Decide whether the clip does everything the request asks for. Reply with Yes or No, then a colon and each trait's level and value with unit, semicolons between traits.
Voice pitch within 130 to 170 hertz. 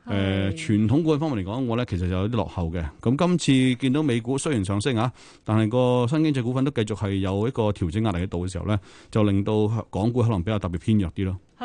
No: low, 110 Hz